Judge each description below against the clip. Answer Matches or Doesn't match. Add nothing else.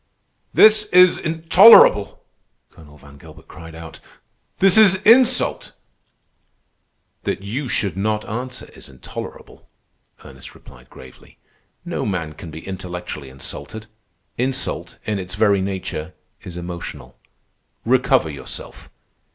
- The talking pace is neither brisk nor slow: Doesn't match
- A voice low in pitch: Matches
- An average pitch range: Doesn't match